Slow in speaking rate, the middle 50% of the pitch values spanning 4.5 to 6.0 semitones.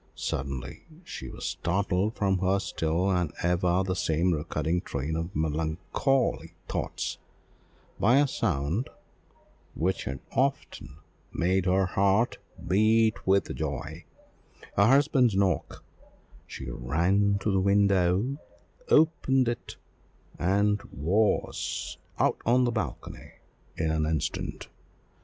Yes: slow, 110 wpm; average, 5.0 semitones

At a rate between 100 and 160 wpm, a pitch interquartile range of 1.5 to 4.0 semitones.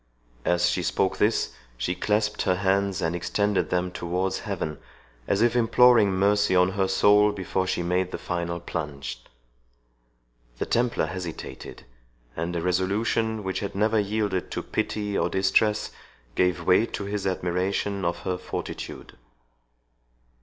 Yes: average, 140 wpm; narrow, 2.6 semitones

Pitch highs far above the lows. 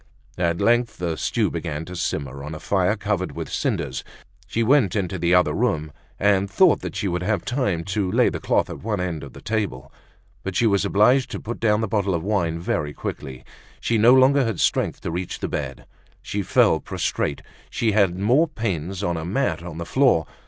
No: average, 4.7 semitones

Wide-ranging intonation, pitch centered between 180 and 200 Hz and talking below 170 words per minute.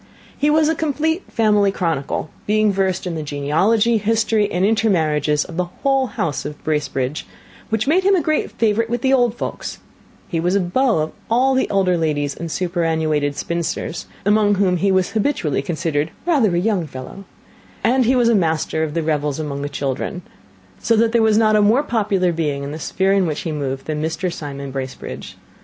No: wide, 6.4 semitones; medium, 185 Hz; average, 195 wpm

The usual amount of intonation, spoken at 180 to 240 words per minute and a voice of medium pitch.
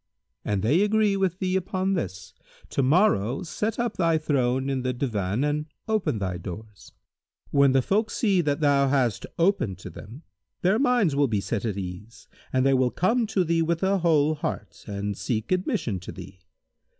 No: wide, 8.9 semitones; average, 185 wpm; medium, 145 Hz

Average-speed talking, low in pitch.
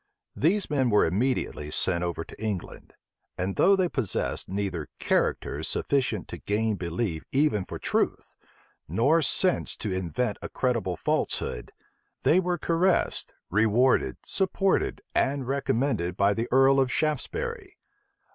No: slow, 130 wpm; low, 125 Hz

